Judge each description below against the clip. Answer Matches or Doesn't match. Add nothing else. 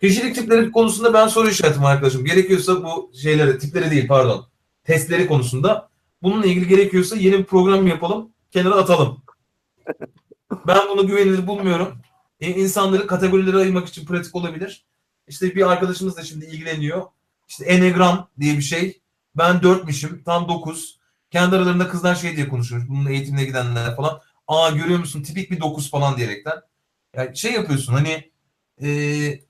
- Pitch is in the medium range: Matches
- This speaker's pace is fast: Matches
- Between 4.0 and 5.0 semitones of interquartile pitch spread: Matches